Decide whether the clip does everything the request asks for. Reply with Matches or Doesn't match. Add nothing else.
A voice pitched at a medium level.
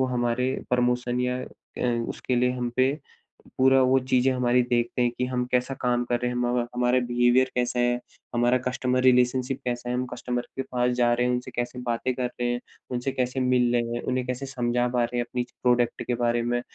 Doesn't match